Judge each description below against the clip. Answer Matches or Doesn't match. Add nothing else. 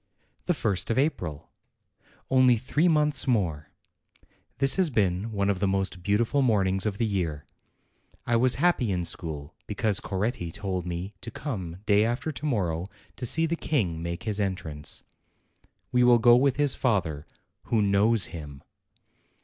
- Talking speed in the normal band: Matches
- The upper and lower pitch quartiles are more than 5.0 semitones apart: Matches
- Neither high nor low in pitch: Doesn't match